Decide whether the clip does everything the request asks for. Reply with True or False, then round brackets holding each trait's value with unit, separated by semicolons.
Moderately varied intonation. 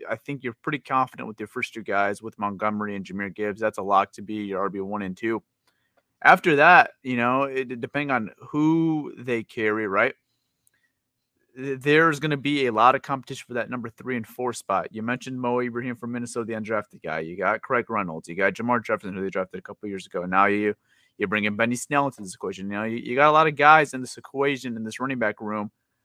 True (3.8 semitones)